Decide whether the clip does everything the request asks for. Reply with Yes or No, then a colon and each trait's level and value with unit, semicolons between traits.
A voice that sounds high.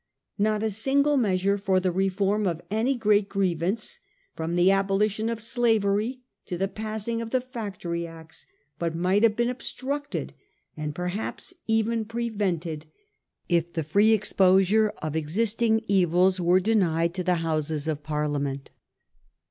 Yes: high, 195 Hz